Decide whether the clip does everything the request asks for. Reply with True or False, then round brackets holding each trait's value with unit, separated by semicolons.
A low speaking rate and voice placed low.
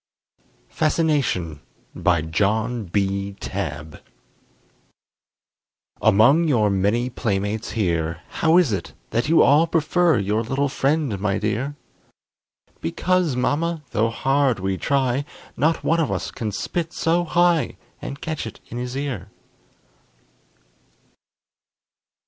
True (115 wpm; 120 Hz)